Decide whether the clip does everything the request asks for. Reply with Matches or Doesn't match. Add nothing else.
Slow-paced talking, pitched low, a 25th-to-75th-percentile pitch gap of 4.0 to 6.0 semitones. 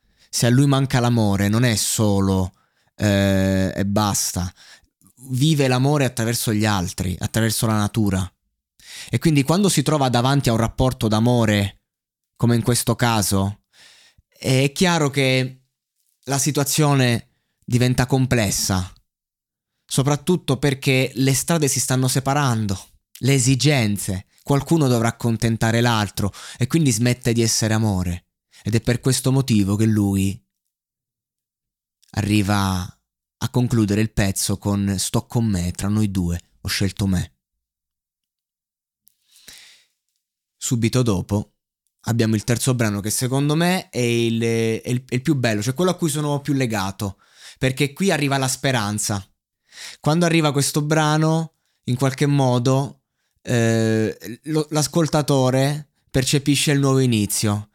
Doesn't match